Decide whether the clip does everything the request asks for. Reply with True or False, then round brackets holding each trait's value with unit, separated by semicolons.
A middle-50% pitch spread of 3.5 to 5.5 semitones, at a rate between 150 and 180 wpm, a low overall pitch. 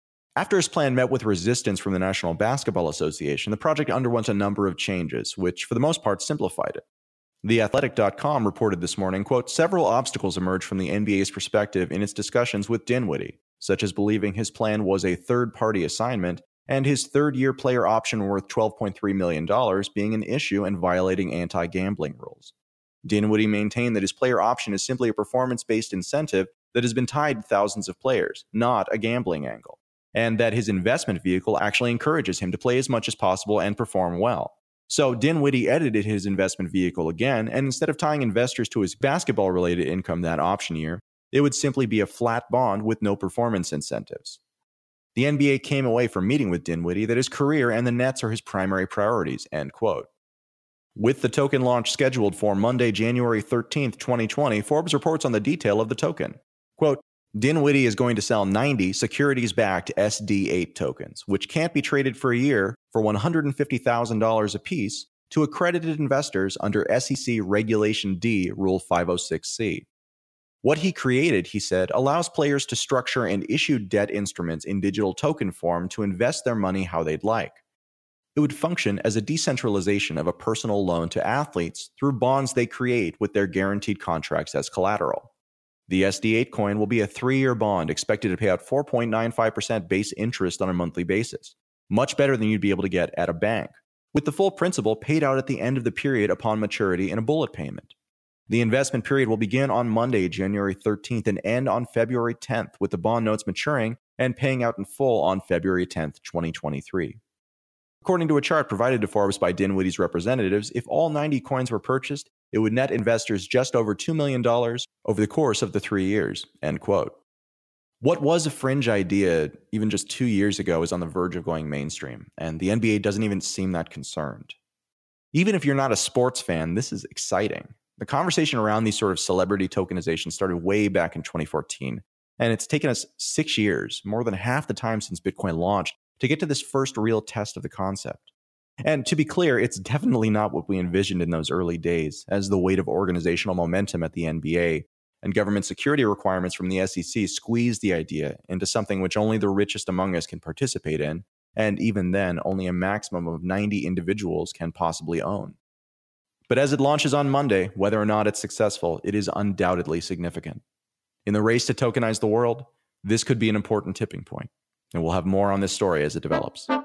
False (5.0 semitones; 190 wpm; 105 Hz)